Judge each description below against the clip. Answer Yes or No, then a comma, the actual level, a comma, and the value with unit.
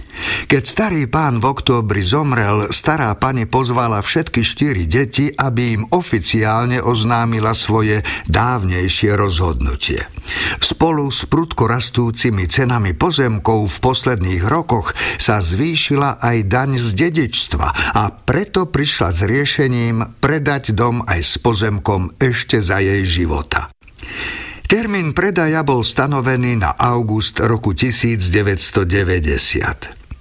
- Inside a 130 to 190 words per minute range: No, slow, 110 wpm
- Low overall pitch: Yes, low, 120 Hz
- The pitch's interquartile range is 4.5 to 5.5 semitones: Yes, average, 4.9 semitones